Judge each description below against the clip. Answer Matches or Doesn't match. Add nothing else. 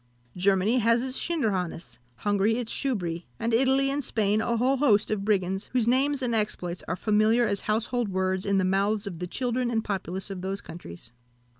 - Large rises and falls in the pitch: Doesn't match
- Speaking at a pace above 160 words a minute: Matches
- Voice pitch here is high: Matches